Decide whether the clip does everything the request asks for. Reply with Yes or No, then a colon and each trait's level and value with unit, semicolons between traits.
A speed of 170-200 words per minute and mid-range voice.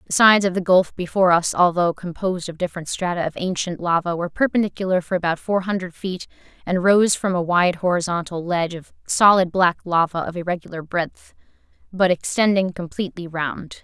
Yes: average, 175 wpm; medium, 180 Hz